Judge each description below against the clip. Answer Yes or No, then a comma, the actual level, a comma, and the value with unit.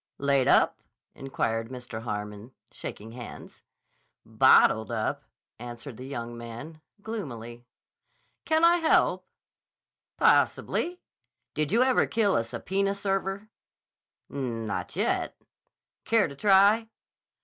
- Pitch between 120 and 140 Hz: Yes, low, 135 Hz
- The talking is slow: Yes, slow, 105 wpm